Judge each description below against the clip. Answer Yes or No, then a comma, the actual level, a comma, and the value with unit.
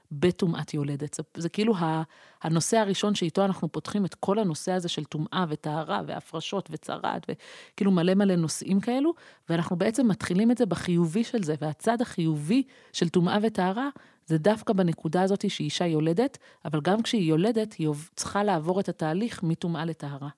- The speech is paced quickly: Yes, fast, 155 wpm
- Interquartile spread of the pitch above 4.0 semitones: Yes, average, 4.5 semitones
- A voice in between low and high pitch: Yes, medium, 180 Hz